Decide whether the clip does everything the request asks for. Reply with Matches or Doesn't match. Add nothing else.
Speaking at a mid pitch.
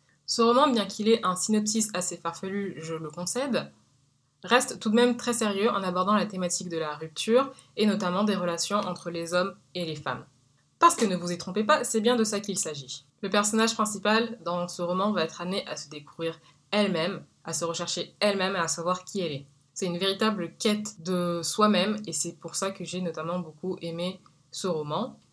Matches